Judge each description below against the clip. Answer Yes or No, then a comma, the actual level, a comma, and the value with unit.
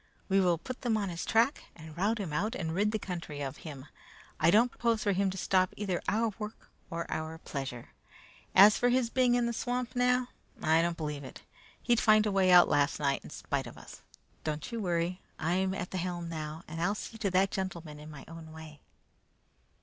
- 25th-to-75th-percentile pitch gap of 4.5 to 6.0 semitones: Yes, average, 5.2 semitones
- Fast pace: Yes, fast, 220 wpm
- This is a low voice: No, medium, 185 Hz